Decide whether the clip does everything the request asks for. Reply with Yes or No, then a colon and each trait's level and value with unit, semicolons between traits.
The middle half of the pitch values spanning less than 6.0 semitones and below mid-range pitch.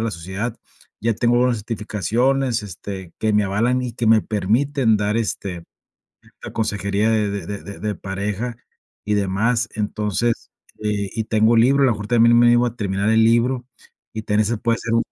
Yes: narrow, 2.5 semitones; low, 110 Hz